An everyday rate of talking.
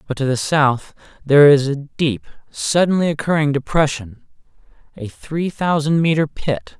No: slow, 130 wpm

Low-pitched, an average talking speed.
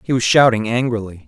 Yes: low, 115 Hz; average, 190 wpm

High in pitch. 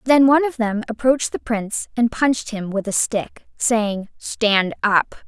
Yes: high, 225 Hz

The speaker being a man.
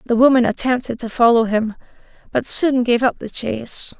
No: female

